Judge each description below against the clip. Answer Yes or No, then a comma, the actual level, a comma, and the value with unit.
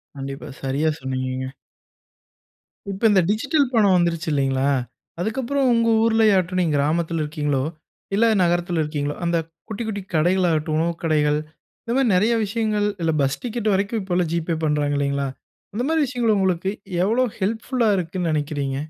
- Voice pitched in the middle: Yes, medium, 175 Hz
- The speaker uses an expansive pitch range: Yes, wide, 6.5 semitones